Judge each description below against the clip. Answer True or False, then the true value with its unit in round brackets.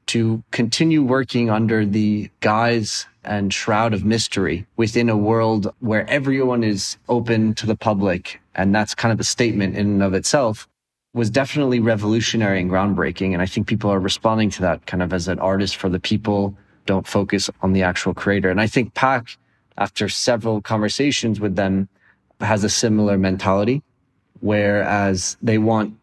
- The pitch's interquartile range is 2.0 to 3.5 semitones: True (2.6 semitones)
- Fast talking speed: False (170 wpm)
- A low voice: True (105 Hz)